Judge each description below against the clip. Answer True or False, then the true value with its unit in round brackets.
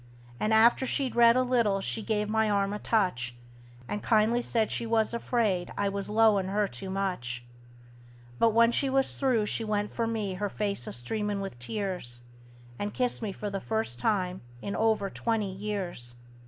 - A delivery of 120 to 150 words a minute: False (180 wpm)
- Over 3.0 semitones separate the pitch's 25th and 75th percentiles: False (2.6 semitones)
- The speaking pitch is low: False (210 Hz)